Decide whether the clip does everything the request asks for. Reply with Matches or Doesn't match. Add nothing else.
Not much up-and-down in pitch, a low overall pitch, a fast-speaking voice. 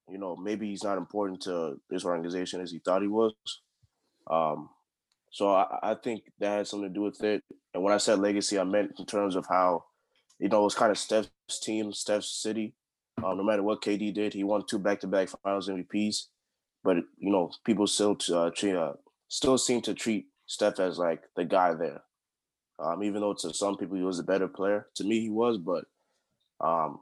Matches